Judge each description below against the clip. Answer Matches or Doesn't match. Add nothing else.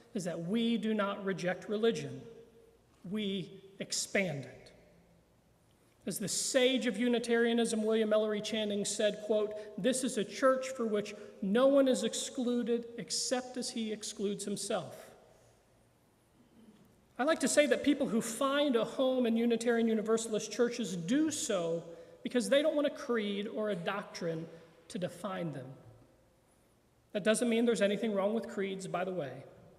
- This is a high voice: Matches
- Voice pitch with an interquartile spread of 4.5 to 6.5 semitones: Doesn't match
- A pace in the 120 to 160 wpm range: Matches